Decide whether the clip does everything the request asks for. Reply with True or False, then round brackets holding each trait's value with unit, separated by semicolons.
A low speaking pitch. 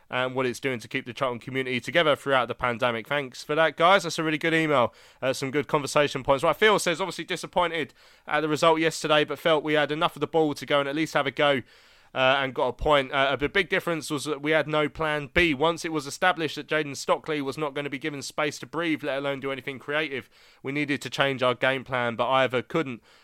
False (150 Hz)